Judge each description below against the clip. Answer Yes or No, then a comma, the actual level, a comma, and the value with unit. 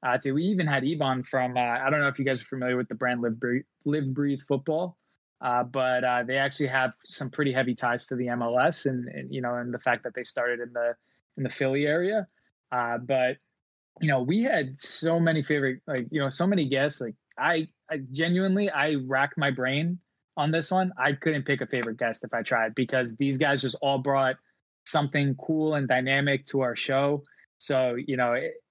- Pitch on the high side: No, low, 135 Hz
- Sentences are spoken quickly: Yes, fast, 220 wpm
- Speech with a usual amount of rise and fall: Yes, average, 3.0 semitones